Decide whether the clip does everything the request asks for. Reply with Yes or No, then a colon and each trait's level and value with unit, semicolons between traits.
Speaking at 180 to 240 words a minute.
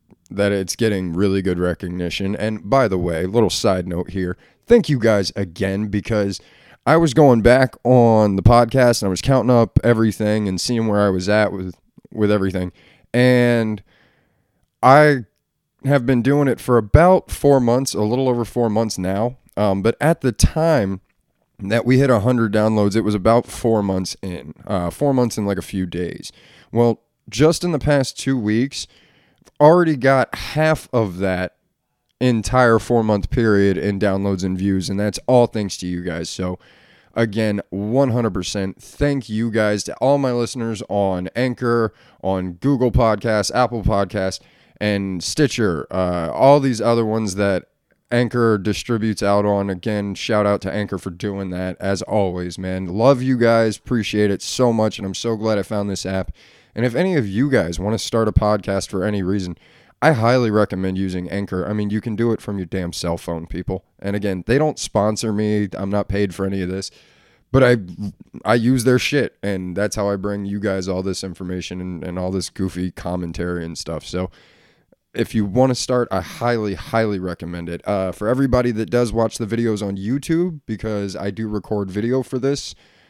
Yes: average, 190 wpm